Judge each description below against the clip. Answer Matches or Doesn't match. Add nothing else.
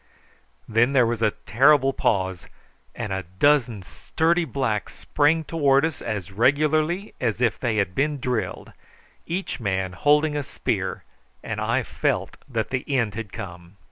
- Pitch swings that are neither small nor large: Doesn't match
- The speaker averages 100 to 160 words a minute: Matches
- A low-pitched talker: Matches